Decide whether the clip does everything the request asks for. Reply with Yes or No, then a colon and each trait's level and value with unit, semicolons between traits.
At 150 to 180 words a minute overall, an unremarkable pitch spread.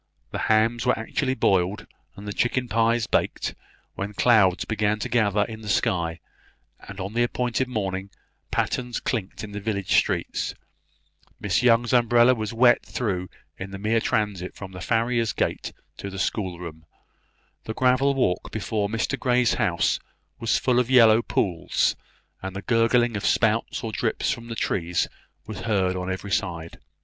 Yes: average, 160 wpm; average, 3.5 semitones